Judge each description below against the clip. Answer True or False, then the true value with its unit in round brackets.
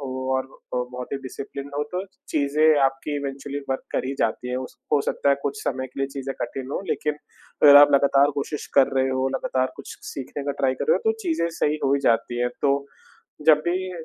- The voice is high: False (140 Hz)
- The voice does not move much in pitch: True (1.7 semitones)